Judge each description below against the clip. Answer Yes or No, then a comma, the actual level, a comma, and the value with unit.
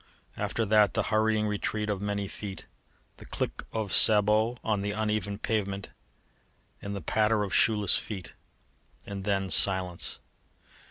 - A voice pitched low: Yes, low, 105 Hz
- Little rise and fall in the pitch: Yes, narrow, 1.5 semitones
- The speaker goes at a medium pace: No, slow, 130 wpm